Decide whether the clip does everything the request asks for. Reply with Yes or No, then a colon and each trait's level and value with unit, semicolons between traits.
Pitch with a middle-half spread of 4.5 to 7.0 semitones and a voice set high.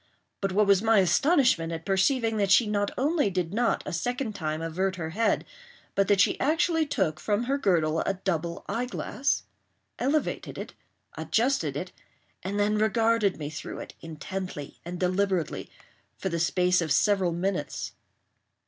Yes: average, 4.8 semitones; high, 195 Hz